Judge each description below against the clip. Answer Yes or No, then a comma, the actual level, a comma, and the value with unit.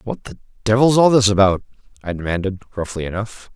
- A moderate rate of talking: Yes, average, 170 wpm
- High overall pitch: No, low, 105 Hz